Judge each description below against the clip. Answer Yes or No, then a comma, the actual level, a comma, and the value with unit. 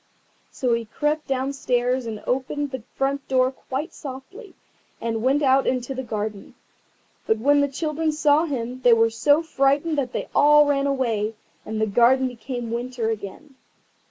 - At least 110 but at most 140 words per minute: No, average, 160 wpm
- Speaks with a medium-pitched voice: No, very high, 260 Hz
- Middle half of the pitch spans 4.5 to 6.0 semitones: No, average, 3.6 semitones